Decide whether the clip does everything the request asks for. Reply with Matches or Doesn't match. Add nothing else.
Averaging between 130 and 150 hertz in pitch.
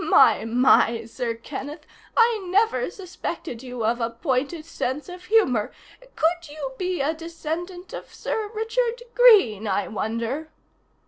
Doesn't match